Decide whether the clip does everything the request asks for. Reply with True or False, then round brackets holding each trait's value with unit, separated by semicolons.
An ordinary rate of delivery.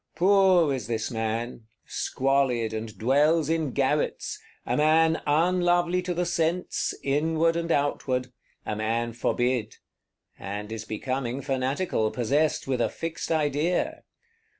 False (115 wpm)